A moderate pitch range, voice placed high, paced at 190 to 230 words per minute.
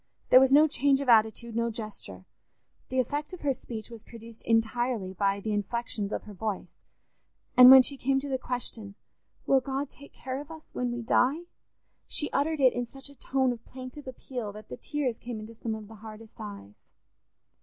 Yes: average, 3.6 semitones; high, 240 Hz; average, 195 wpm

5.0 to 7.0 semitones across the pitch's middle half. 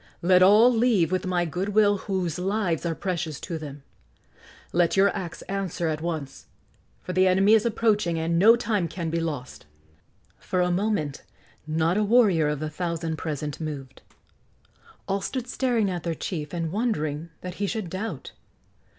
No: average, 4.0 semitones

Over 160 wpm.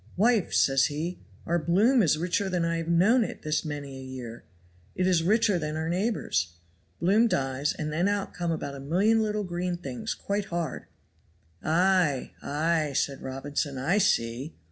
Yes: average, 170 wpm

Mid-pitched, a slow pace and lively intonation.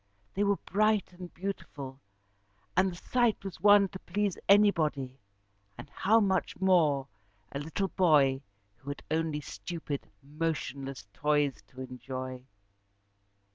Yes: medium, 165 Hz; slow, 125 wpm; wide, 5.8 semitones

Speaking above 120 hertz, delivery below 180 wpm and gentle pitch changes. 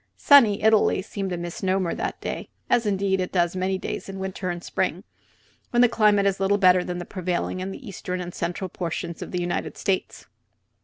No: high, 190 Hz; average, 200 wpm; narrow, 1.9 semitones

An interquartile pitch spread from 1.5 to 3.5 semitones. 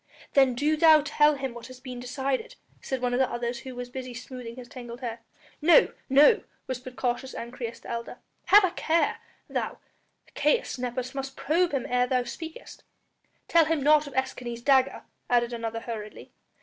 Yes: average, 3.0 semitones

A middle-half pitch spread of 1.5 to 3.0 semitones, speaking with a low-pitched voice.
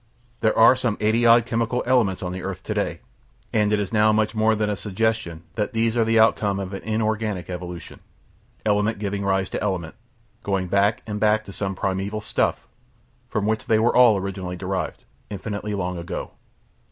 Yes: narrow, 2.4 semitones; low, 105 Hz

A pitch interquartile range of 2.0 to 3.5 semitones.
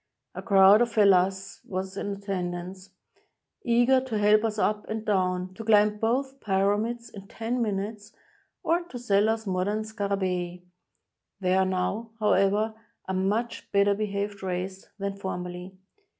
Yes: narrow, 2.5 semitones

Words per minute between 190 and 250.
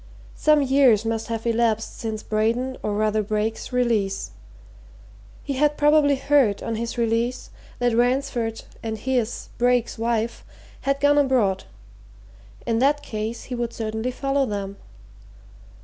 No: slow, 135 wpm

